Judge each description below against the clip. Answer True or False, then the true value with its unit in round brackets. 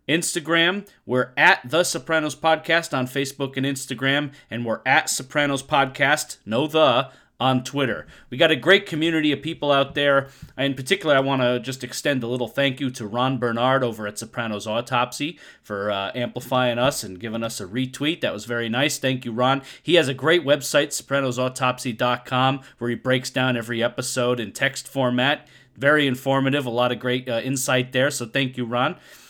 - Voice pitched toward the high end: False (130 Hz)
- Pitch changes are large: False (2.9 semitones)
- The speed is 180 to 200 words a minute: True (185 wpm)